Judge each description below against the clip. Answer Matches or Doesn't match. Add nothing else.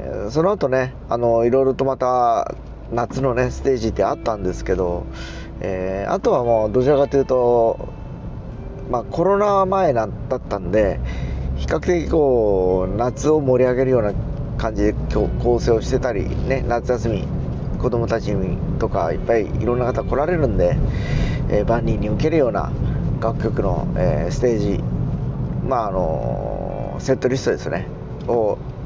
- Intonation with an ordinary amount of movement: Matches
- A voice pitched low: Matches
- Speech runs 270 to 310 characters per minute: Matches